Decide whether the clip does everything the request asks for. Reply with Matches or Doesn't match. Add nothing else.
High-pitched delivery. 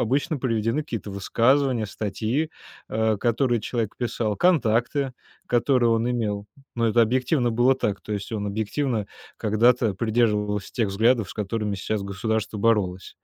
Doesn't match